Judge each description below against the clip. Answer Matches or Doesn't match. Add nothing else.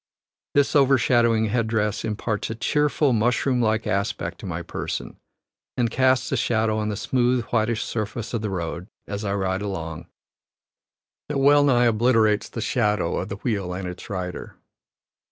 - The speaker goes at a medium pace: Matches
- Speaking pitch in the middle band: Doesn't match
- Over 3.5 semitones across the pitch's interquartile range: Doesn't match